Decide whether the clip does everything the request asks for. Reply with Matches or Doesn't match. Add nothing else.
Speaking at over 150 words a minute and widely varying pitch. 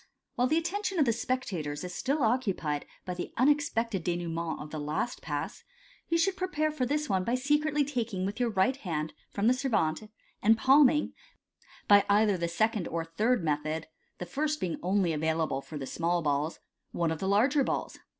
Matches